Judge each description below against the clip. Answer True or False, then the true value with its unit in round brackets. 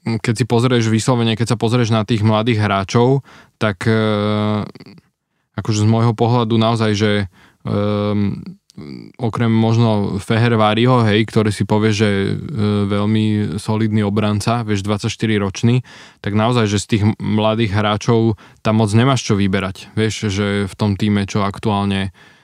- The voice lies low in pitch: True (110 Hz)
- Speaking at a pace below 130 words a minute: False (145 wpm)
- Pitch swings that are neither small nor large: False (1.7 semitones)